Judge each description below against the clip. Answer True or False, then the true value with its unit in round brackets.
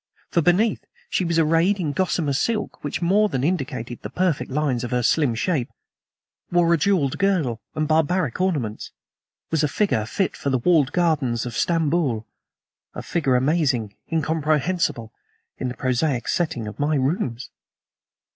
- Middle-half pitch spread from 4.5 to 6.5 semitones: True (5.3 semitones)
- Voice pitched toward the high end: False (150 Hz)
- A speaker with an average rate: True (155 wpm)